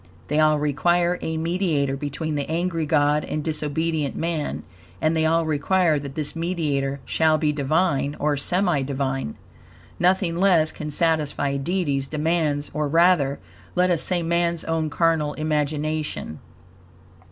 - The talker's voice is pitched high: No, medium, 155 Hz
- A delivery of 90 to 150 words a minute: Yes, average, 140 wpm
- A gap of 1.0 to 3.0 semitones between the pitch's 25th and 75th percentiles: Yes, narrow, 2.5 semitones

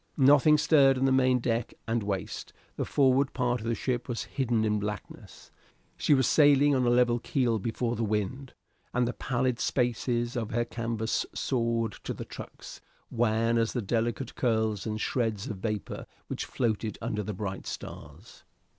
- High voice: No, low, 120 Hz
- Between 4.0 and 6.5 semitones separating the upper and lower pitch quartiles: No, narrow, 2.6 semitones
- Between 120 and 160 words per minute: No, average, 170 wpm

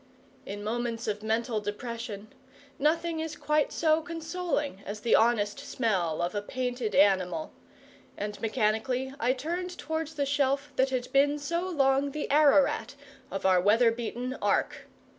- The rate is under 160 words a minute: Yes, average, 145 wpm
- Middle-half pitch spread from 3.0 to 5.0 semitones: No, wide, 5.4 semitones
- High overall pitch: Yes, very high, 250 Hz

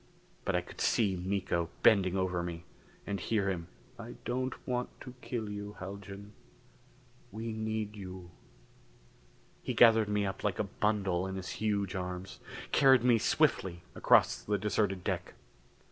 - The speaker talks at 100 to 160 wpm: Yes, average, 145 wpm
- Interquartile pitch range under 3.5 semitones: Yes, average, 2.8 semitones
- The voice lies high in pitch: No, low, 100 Hz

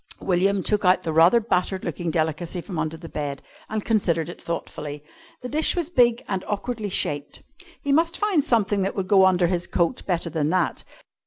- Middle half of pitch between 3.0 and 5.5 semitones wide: Yes, average, 4.6 semitones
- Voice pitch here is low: No, medium, 185 Hz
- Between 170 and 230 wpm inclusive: Yes, average, 190 wpm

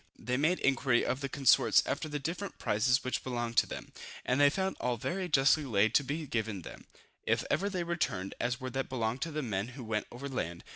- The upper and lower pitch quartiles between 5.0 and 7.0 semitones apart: No, average, 4.0 semitones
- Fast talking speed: Yes, fast, 230 wpm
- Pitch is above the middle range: No, low, 130 Hz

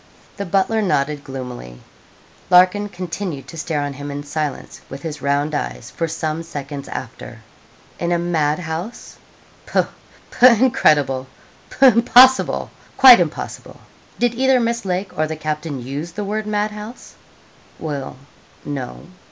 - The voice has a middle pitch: Yes, medium, 165 Hz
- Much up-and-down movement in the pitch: Yes, wide, 6.3 semitones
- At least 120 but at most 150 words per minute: Yes, average, 140 wpm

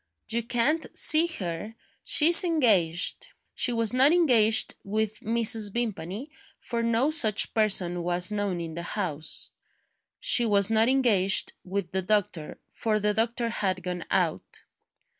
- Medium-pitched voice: No, high, 215 Hz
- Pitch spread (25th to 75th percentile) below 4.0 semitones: No, average, 4.3 semitones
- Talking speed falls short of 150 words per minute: Yes, average, 140 wpm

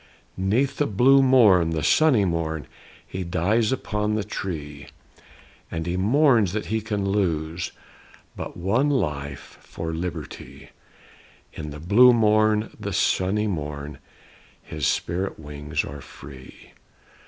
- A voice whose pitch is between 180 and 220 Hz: No, very low, 95 Hz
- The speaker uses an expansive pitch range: Yes, wide, 5.8 semitones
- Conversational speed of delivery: No, slow, 130 wpm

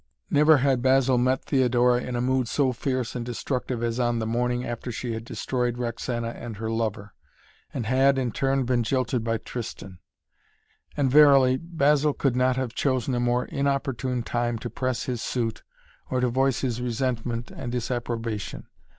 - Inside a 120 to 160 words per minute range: No, average, 170 wpm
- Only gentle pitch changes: Yes, narrow, 2.0 semitones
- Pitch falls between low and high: No, low, 125 Hz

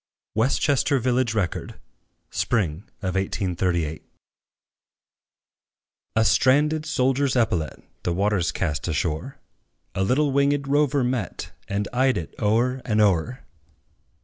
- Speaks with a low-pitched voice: Yes, low, 115 Hz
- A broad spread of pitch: Yes, wide, 6.2 semitones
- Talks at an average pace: No, slow, 105 wpm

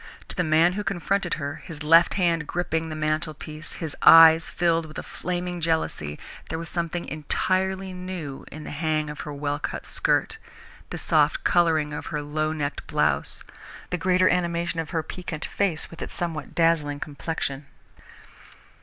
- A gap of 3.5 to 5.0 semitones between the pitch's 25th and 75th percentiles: No, narrow, 2.4 semitones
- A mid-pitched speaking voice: Yes, medium, 165 Hz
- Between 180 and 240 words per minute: No, average, 165 wpm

